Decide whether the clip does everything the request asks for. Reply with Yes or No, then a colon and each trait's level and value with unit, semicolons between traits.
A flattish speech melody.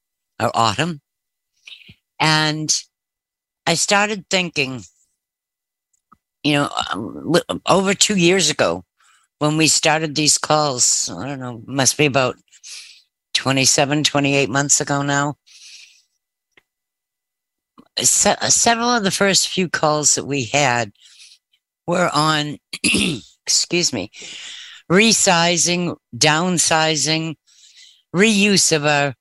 No: average, 3.8 semitones